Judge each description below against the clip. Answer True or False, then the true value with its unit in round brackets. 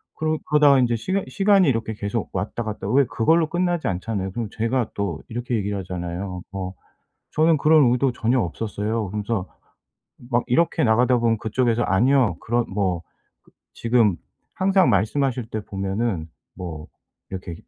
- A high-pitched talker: False (115 Hz)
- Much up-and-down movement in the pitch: False (5.0 semitones)